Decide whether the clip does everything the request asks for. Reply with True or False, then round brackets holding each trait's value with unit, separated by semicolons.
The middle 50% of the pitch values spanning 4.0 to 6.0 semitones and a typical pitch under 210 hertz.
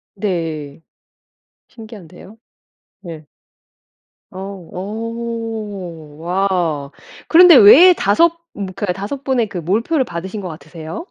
True (5.1 semitones; 195 Hz)